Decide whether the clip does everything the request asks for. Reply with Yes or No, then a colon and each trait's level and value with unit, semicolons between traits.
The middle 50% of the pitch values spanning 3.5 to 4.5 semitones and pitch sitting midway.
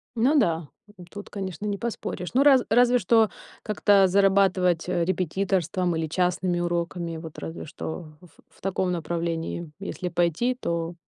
No: average, 2.9 semitones; medium, 180 Hz